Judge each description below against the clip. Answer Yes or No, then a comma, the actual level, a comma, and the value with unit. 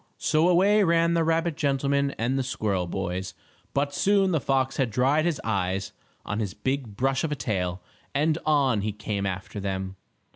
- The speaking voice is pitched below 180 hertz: Yes, low, 135 Hz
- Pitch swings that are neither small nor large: No, wide, 7.6 semitones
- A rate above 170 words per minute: Yes, average, 180 wpm